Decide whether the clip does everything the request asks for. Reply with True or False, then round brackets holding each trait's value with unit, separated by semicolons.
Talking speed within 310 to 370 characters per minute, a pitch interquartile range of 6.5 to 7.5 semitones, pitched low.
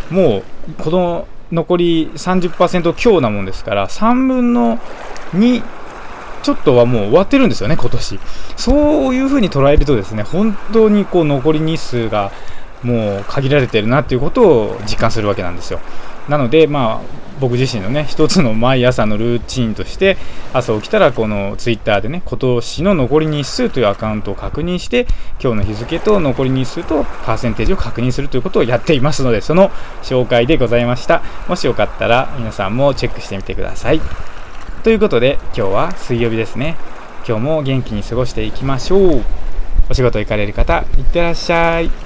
True (340 characters per minute; 6.9 semitones; 130 Hz)